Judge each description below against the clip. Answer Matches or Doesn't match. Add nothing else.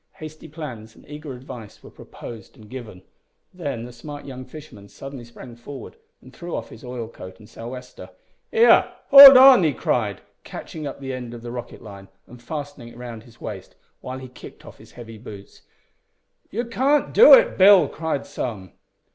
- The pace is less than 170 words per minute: Doesn't match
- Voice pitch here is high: Doesn't match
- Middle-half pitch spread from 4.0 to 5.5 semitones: Matches